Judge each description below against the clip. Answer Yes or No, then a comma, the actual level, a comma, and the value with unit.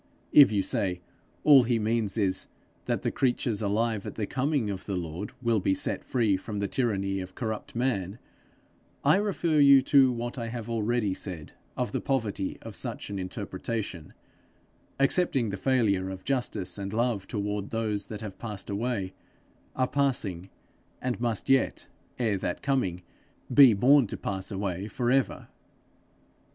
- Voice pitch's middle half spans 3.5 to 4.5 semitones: Yes, average, 4.2 semitones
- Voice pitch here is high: No, low, 110 Hz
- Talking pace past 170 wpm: No, average, 160 wpm